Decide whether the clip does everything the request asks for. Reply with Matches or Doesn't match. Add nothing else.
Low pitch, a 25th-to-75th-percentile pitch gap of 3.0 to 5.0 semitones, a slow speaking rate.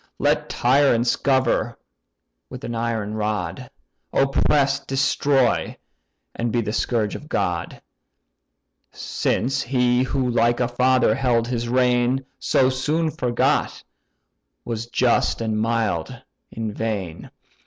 Doesn't match